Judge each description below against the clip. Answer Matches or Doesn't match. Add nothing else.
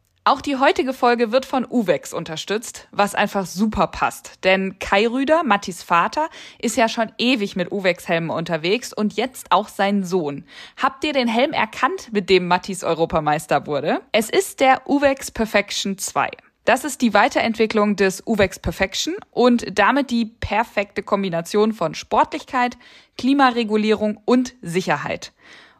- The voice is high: Matches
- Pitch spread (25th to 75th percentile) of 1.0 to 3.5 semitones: Doesn't match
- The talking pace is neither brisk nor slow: Matches